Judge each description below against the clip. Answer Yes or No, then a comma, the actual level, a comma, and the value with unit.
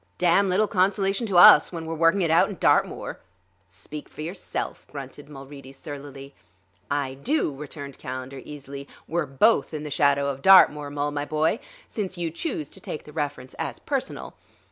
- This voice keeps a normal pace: Yes, average, 170 wpm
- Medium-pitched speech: Yes, medium, 150 Hz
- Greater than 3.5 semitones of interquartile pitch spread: Yes, average, 3.9 semitones